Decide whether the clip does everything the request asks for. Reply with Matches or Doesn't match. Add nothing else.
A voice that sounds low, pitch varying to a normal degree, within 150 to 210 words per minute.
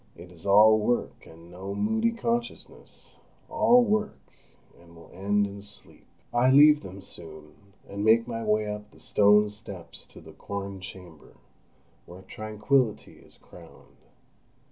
Doesn't match